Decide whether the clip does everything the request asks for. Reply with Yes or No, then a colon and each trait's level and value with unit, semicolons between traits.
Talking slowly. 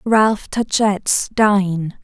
Yes: slow, 90 wpm